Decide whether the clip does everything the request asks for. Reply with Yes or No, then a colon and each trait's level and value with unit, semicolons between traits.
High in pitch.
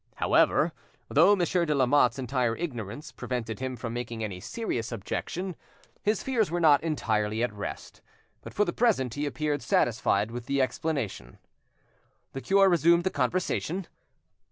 No: low, 135 Hz